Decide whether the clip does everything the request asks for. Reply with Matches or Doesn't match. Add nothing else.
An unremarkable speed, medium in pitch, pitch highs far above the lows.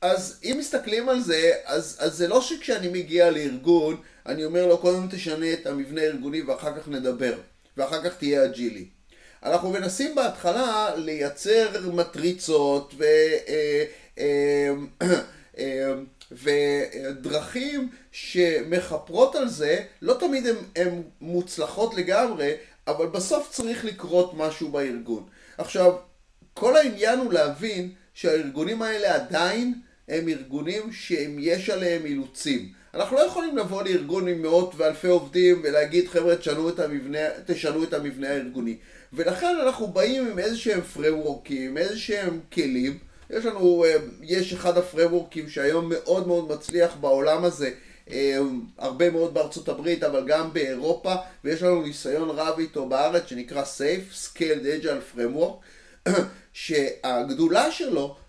Matches